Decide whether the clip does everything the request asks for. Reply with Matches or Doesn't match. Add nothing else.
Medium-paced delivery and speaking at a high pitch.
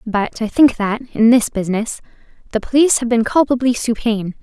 Matches